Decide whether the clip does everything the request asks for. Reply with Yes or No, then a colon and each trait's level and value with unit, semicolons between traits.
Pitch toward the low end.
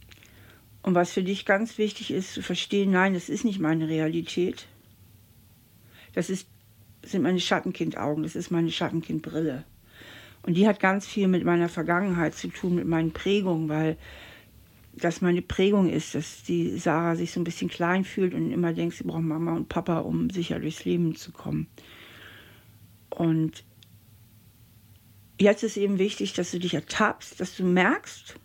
No: medium, 165 Hz